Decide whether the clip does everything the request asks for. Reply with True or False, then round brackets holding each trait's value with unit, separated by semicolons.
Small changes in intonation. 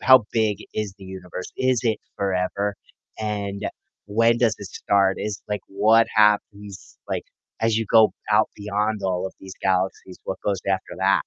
True (2.2 semitones)